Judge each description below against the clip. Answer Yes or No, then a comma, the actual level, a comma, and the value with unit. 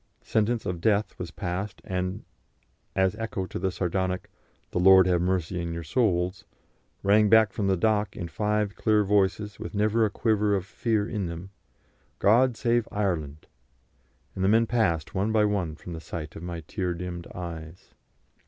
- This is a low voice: Yes, very low, 95 Hz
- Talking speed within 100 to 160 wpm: No, average, 170 wpm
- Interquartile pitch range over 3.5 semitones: No, average, 3.2 semitones